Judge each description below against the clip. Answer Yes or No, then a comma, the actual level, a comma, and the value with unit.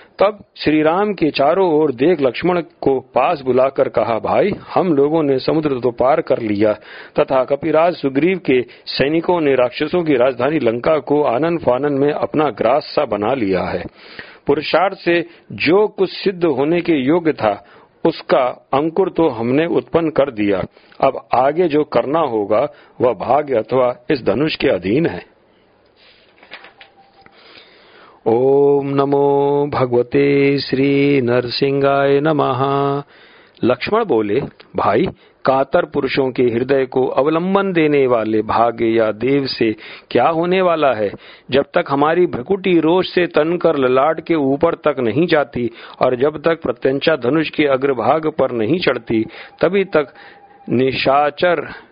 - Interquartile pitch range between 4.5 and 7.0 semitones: No, average, 3.8 semitones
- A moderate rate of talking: Yes, average, 140 wpm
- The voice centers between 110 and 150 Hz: Yes, medium, 140 Hz